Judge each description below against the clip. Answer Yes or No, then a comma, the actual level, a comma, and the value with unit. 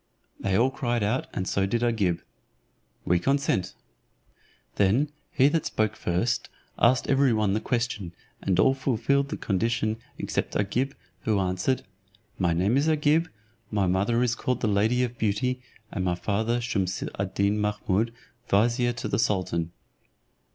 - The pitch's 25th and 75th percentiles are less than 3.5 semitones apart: No, average, 4.3 semitones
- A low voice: Yes, low, 110 Hz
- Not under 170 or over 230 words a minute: No, average, 150 wpm